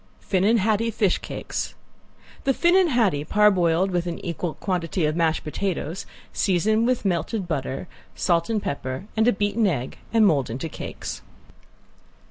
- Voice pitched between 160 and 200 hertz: Yes, medium, 185 Hz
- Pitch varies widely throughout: No, average, 4.7 semitones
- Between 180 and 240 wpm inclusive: No, average, 145 wpm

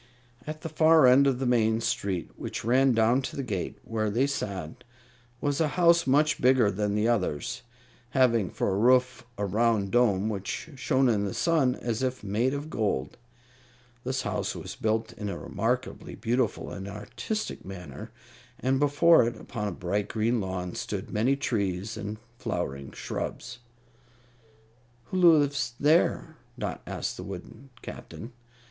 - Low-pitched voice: Yes, low, 120 Hz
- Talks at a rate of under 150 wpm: No, average, 155 wpm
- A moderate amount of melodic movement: Yes, average, 4.6 semitones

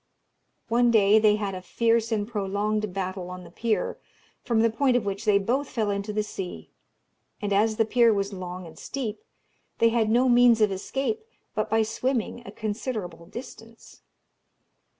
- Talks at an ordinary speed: Yes, average, 170 wpm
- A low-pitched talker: No, high, 215 Hz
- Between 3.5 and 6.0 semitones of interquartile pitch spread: No, average, 2.8 semitones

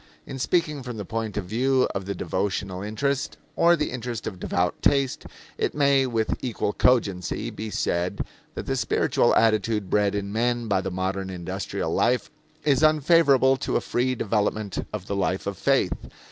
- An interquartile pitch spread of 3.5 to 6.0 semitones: Yes, average, 5.2 semitones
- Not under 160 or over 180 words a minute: Yes, average, 175 wpm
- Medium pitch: No, low, 110 Hz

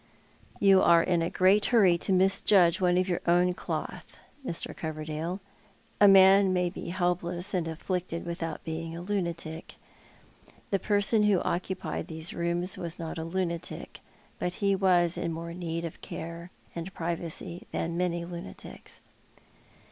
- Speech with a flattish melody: Yes, narrow, 1.9 semitones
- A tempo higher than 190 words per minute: No, average, 150 wpm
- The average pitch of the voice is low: No, medium, 175 Hz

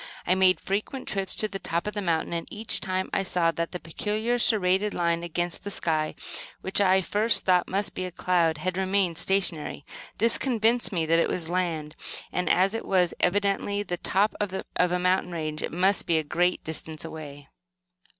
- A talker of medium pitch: Yes, medium, 180 Hz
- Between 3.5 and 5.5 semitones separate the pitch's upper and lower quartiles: No, average, 3.0 semitones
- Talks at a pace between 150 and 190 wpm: No, average, 200 wpm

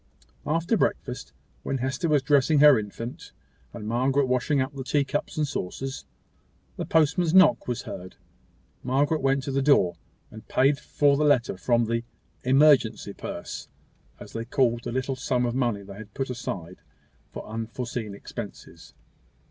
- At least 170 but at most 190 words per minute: No, average, 155 wpm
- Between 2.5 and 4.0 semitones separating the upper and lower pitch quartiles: Yes, average, 3.5 semitones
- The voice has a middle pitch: No, low, 130 Hz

